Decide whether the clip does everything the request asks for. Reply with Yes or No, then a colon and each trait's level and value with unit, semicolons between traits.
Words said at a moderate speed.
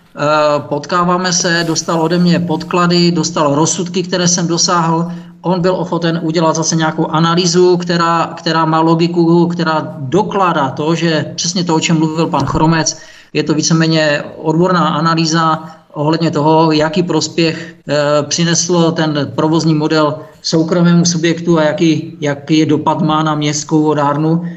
Yes: average, 140 wpm